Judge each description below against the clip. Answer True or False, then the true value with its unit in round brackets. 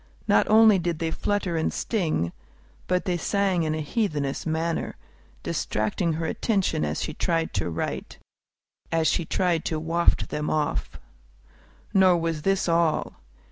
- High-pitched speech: False (165 Hz)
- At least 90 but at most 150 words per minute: True (145 wpm)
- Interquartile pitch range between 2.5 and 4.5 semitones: True (2.8 semitones)